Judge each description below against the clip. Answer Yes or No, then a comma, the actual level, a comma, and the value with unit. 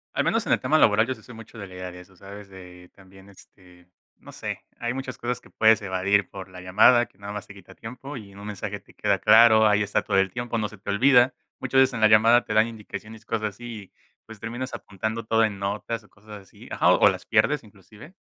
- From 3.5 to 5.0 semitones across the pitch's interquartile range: No, average, 2.9 semitones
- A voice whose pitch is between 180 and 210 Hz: No, low, 105 Hz